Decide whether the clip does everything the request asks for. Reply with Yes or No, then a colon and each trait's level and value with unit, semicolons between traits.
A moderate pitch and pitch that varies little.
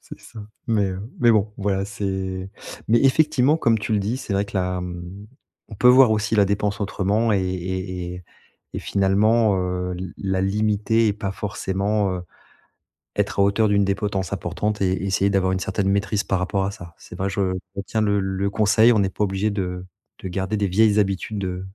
No: low, 100 Hz; narrow, 2.1 semitones